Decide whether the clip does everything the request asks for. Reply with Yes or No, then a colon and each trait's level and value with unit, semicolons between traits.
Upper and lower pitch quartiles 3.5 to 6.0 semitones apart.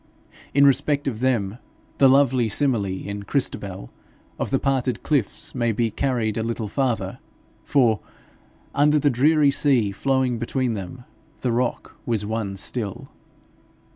Yes: average, 3.9 semitones